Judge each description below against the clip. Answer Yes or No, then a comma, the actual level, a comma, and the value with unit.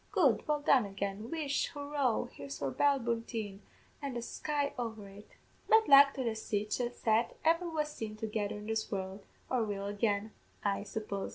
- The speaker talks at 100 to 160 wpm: No, average, 175 wpm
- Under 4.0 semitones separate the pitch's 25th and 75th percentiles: No, average, 5.3 semitones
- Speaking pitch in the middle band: No, high, 225 Hz